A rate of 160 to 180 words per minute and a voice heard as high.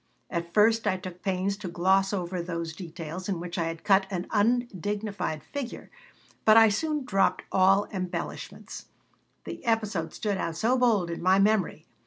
Yes: average, 165 wpm; high, 195 Hz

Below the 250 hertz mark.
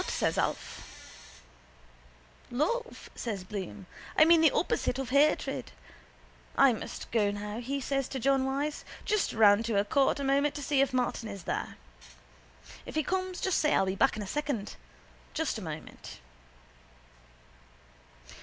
No: very high, 270 Hz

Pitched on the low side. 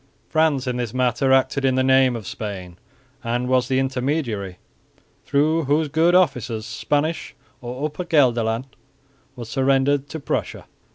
Yes: low, 130 Hz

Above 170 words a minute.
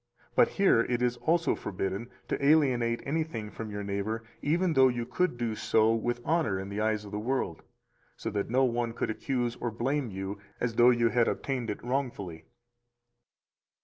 Yes: average, 180 wpm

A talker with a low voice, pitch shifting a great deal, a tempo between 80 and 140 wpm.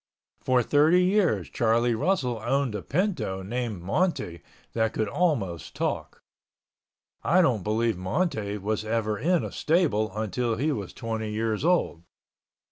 Yes: low, 115 Hz; wide, 6.3 semitones; slow, 135 wpm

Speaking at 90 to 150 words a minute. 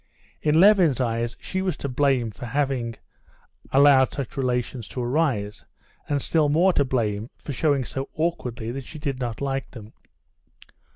No: average, 160 wpm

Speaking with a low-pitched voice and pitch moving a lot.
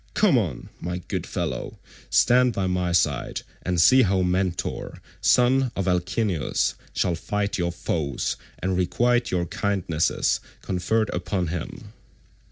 No: very low, 90 Hz; average, 3.7 semitones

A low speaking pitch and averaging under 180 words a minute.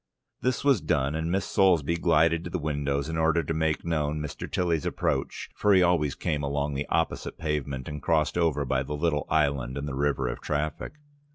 No: very low, 75 Hz; average, 200 wpm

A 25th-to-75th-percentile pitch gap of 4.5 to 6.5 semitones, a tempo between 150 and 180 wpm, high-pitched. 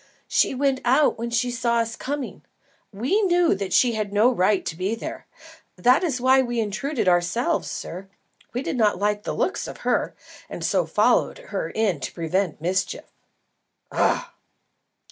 Yes: average, 5.0 semitones; average, 165 wpm; high, 235 Hz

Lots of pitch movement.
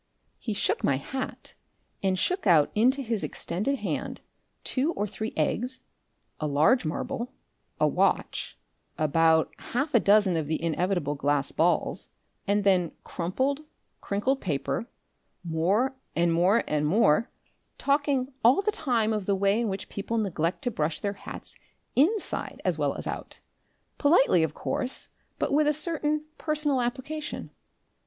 Yes: wide, 7.9 semitones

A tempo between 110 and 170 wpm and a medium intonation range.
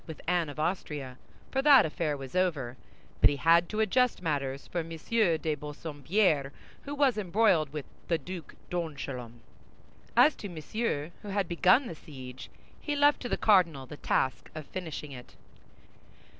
No: average, 155 wpm; wide, 5.7 semitones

